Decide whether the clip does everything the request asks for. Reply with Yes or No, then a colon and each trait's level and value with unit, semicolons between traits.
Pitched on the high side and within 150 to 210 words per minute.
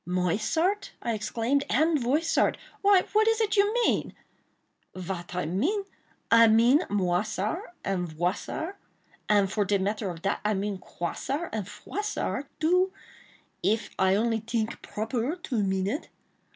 No: high, 225 Hz; average, 140 wpm